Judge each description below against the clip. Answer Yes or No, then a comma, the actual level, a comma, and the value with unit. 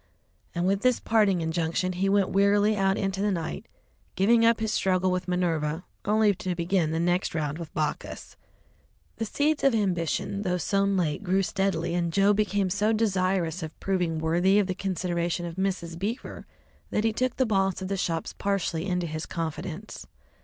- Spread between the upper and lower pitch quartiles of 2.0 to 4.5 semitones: Yes, average, 3.0 semitones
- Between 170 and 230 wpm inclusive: Yes, average, 180 wpm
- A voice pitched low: No, medium, 185 Hz